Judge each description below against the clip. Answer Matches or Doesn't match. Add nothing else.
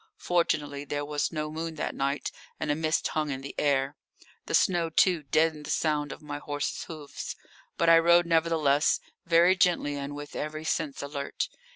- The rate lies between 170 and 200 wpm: Matches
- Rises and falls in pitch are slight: Matches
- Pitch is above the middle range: Doesn't match